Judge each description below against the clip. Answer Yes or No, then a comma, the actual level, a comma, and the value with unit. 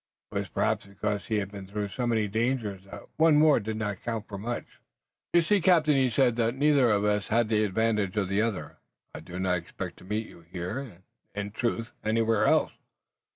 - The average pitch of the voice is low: Yes, low, 110 Hz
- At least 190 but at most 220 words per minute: Yes, average, 200 wpm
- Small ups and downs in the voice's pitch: No, average, 3.2 semitones